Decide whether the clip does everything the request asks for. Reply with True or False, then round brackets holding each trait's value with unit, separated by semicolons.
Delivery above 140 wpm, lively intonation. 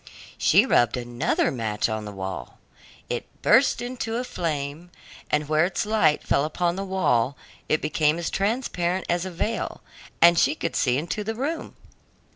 True (165 wpm; 6.0 semitones)